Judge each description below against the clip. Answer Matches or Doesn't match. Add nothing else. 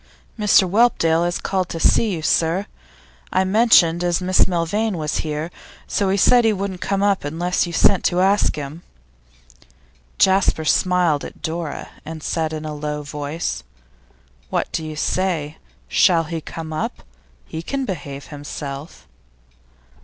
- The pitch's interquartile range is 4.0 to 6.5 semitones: Doesn't match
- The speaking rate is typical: Matches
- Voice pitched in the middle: Matches